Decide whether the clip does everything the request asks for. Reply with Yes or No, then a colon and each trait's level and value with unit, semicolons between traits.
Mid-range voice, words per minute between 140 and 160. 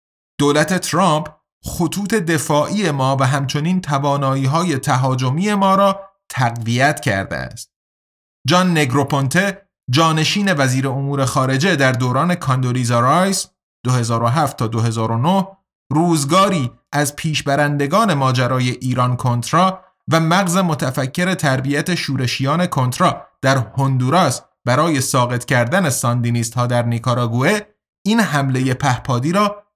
No: medium, 145 Hz; slow, 105 wpm